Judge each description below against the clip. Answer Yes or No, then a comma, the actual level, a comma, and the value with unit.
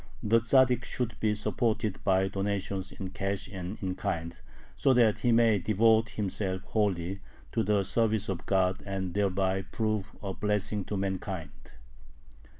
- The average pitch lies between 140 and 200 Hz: No, low, 100 Hz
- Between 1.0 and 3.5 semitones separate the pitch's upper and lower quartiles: Yes, narrow, 2.4 semitones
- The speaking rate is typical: Yes, average, 150 wpm